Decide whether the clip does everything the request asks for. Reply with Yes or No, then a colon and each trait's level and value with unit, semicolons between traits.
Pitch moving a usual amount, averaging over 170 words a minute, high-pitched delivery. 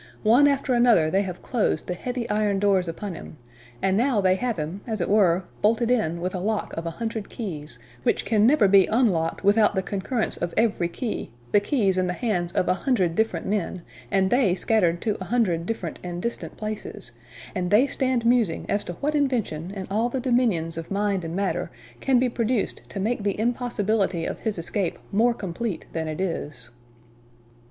Yes: average, 4.6 semitones; average, 195 wpm; high, 205 Hz